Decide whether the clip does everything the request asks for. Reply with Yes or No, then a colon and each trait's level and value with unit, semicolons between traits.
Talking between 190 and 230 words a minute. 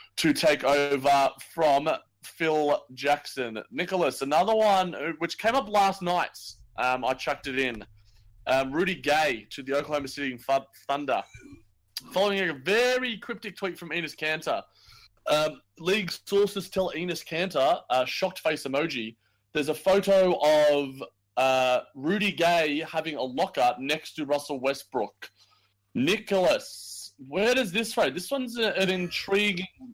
No: slow, 135 wpm